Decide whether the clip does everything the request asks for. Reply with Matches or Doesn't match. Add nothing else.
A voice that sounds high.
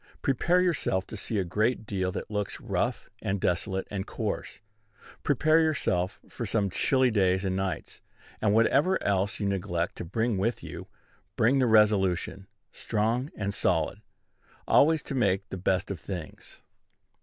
Doesn't match